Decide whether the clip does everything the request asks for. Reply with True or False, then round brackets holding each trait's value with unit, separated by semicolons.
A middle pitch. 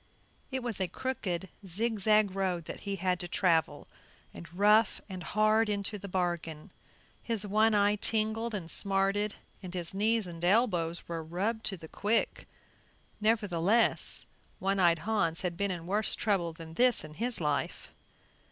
False (195 Hz)